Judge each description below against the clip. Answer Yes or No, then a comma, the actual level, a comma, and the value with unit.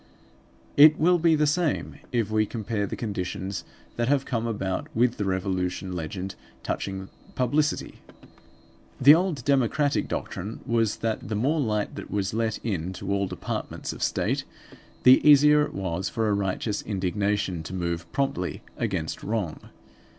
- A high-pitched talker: No, low, 105 Hz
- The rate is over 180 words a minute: No, average, 150 wpm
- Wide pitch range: Yes, wide, 5.7 semitones